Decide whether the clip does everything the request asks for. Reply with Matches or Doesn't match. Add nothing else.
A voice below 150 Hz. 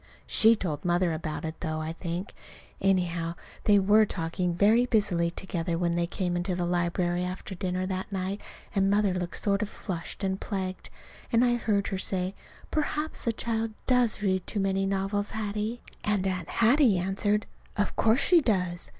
Doesn't match